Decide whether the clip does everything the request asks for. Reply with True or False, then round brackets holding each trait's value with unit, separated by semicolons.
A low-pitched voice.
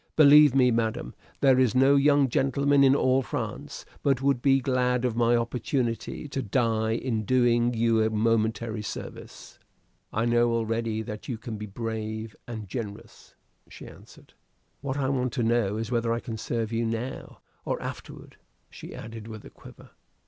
True (120 Hz)